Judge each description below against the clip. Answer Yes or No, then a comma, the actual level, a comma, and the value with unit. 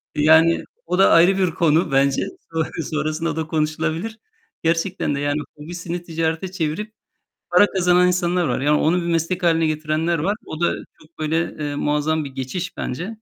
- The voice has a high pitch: No, medium, 165 Hz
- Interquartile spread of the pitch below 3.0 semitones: Yes, narrow, 2.5 semitones